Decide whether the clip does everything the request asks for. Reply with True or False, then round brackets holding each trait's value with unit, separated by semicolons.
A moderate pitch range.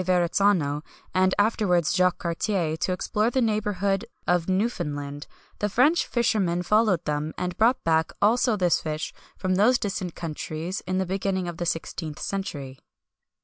True (4.0 semitones)